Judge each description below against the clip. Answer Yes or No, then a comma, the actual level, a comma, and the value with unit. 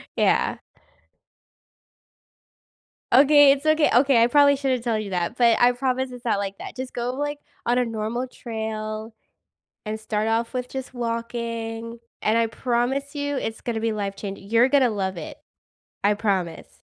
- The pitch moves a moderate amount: Yes, average, 3.0 semitones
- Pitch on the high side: Yes, high, 235 Hz